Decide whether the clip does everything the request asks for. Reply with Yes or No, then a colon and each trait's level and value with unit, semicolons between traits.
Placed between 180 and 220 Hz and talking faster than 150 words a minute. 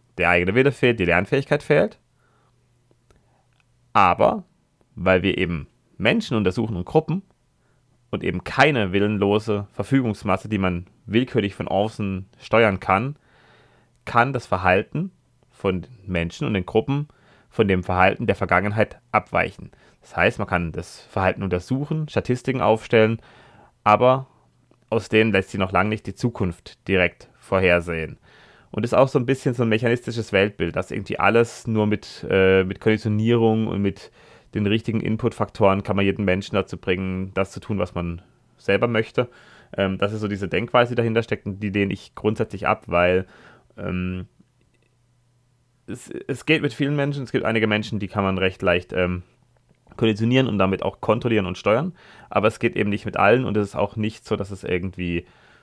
No: low, 110 Hz; average, 165 wpm